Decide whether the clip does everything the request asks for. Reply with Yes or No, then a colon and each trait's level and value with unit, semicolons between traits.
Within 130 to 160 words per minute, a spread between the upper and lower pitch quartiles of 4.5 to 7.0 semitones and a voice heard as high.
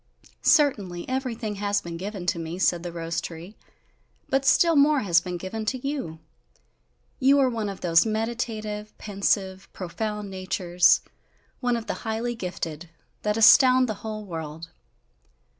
Yes: average, 145 wpm; average, 5.0 semitones; high, 210 Hz